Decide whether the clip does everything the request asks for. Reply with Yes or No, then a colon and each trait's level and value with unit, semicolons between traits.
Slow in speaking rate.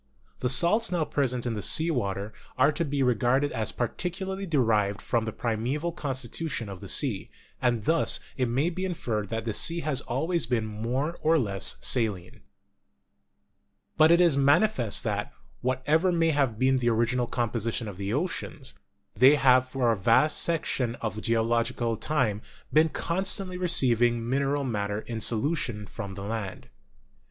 No: average, 160 wpm